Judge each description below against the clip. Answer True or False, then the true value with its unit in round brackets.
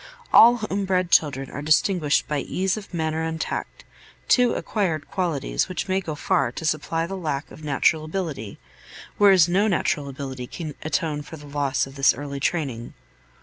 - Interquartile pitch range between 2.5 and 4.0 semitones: False (4.4 semitones)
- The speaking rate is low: False (175 wpm)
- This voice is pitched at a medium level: True (155 Hz)